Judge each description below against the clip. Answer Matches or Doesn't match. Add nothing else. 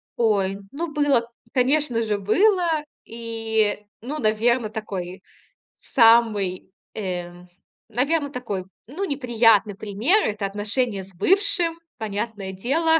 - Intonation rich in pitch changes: Matches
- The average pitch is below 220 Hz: Doesn't match